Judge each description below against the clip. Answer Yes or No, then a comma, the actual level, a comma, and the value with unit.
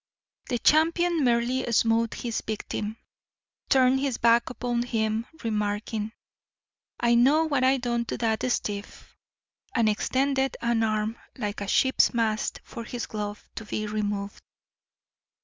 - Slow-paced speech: Yes, slow, 130 wpm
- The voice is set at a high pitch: Yes, high, 235 Hz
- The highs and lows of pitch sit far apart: No, average, 2.9 semitones